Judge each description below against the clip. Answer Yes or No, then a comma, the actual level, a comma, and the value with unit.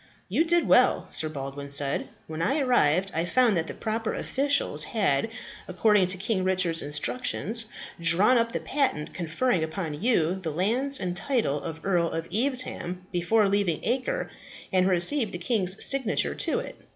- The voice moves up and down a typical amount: No, wide, 6.3 semitones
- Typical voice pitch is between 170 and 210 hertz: Yes, high, 190 Hz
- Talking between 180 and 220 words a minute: No, average, 165 wpm